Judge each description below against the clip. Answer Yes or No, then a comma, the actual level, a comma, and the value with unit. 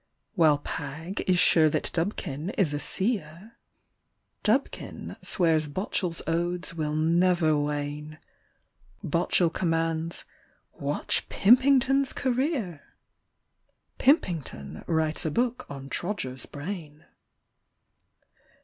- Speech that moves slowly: Yes, slow, 100 wpm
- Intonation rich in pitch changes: No, average, 4.6 semitones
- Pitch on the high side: No, medium, 165 Hz